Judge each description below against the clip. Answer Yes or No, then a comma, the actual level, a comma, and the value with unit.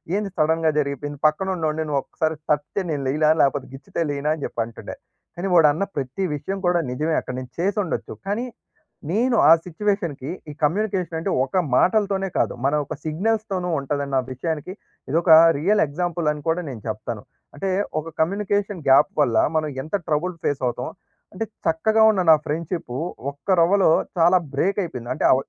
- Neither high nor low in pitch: Yes, medium, 160 Hz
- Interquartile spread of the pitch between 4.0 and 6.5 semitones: Yes, average, 4.9 semitones